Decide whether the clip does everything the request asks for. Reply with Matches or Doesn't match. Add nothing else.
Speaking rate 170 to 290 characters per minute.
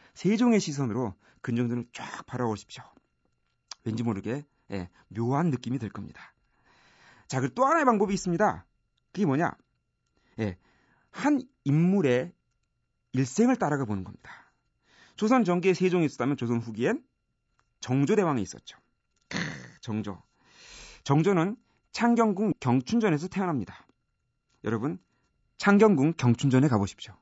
Matches